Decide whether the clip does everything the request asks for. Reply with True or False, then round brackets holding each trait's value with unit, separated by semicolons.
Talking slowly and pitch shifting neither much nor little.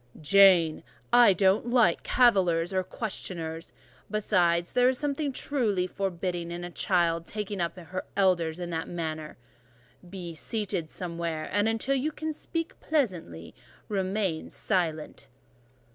True (130 wpm; 4.1 semitones)